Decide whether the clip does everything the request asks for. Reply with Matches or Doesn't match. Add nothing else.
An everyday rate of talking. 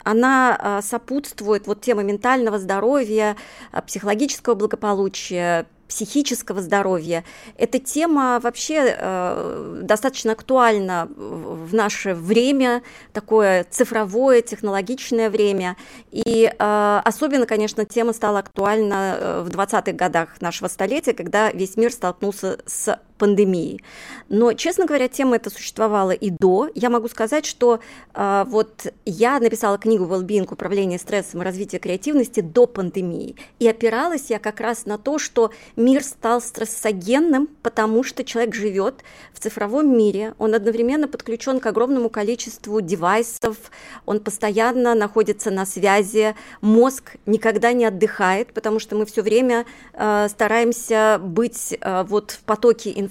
Matches